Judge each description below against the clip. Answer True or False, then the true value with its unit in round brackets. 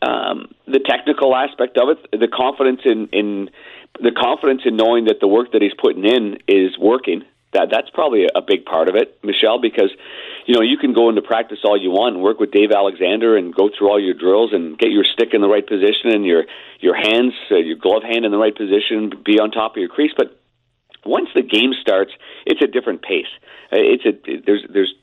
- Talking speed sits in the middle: False (225 wpm)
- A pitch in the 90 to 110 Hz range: False (130 Hz)